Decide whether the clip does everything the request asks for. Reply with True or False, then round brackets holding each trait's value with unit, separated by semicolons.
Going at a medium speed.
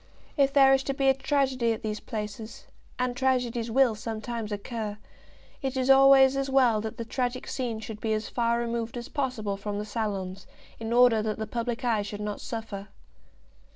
True (190 wpm)